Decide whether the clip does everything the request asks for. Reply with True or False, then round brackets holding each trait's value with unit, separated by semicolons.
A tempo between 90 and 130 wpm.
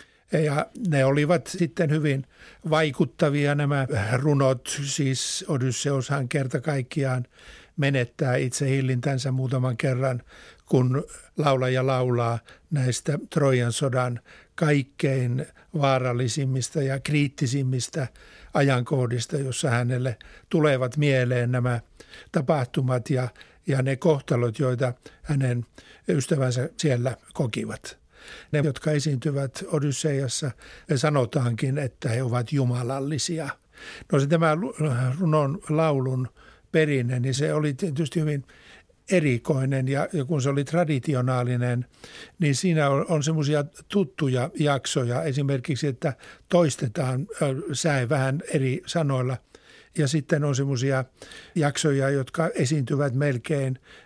True (105 wpm)